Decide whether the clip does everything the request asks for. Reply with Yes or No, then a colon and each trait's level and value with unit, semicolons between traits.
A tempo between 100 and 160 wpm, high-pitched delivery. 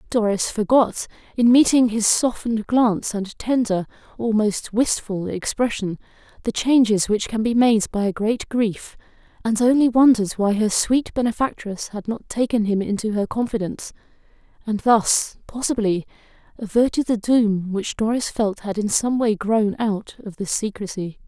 Yes: average, 150 wpm; high, 220 Hz